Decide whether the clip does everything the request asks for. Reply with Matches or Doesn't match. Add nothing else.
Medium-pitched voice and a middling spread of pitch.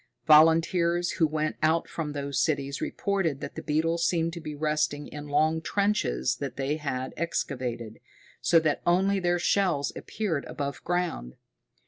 Matches